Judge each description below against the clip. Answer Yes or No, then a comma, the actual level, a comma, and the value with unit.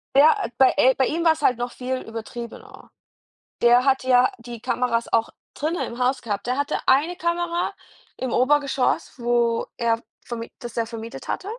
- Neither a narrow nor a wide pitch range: Yes, average, 3.3 semitones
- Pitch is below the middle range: No, very high, 250 Hz